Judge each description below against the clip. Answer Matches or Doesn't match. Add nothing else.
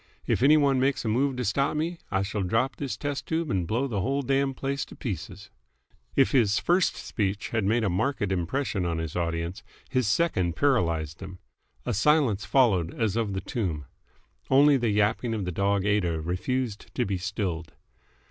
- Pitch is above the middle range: Doesn't match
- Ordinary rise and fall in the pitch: Doesn't match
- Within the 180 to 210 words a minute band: Matches